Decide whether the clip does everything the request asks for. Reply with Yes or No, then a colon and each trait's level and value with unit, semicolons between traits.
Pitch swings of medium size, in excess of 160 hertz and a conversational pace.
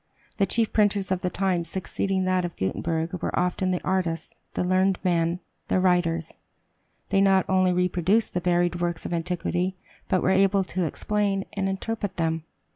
No: narrow, 1.8 semitones; medium, 185 Hz; average, 170 wpm